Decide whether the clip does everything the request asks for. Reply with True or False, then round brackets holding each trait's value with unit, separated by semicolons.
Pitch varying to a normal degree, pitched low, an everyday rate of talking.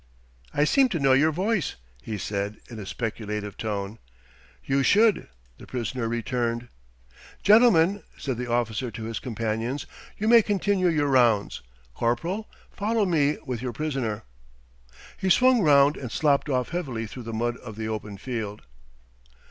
False (6.7 semitones; 125 Hz; 150 wpm)